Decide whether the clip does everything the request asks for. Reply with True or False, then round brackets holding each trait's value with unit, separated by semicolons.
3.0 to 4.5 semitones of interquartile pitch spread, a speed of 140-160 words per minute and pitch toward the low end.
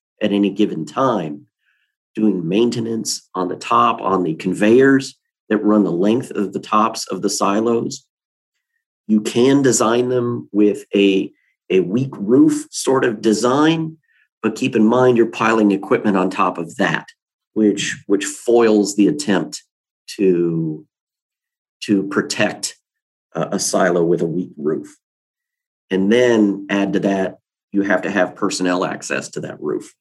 True (4.0 semitones; 150 wpm; 110 Hz)